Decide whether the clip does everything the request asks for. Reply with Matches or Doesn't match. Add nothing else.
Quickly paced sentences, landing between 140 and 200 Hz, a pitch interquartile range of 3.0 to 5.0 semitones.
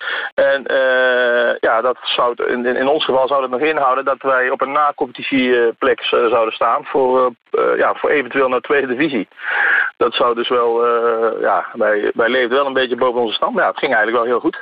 Doesn't match